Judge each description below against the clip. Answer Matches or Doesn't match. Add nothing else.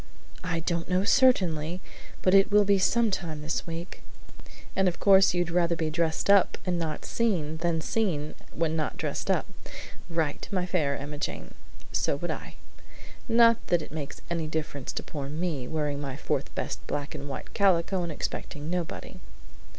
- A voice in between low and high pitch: Matches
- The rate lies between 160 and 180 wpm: Matches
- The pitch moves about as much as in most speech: Matches